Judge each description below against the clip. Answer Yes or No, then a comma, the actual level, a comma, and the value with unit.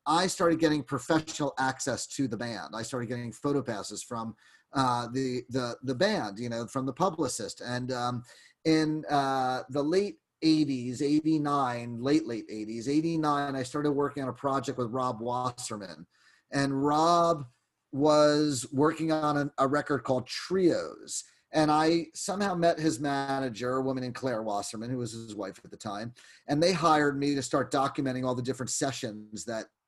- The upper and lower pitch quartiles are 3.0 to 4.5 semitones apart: Yes, average, 3.5 semitones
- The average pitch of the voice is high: No, low, 135 Hz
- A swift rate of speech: No, average, 170 wpm